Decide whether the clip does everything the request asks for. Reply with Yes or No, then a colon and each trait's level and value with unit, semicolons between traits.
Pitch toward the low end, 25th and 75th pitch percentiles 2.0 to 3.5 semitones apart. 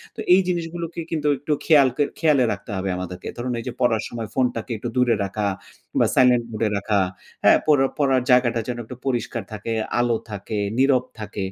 No: low, 125 Hz; average, 3.9 semitones